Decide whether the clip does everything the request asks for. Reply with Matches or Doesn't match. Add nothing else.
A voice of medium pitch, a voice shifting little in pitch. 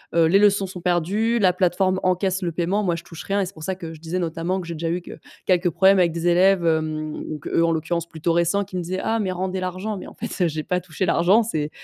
Matches